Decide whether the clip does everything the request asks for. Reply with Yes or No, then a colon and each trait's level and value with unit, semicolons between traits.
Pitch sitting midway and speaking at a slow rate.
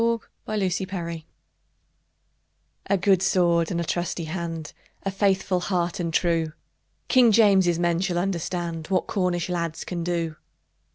Yes: medium, 175 Hz; slow, 125 wpm